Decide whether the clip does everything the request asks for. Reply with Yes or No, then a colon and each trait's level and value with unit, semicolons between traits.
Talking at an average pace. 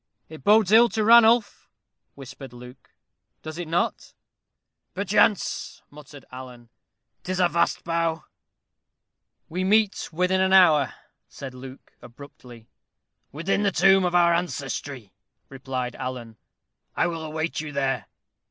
No: slow, 125 wpm